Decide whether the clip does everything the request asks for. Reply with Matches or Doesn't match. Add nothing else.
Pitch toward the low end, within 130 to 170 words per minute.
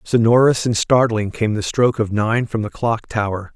Doesn't match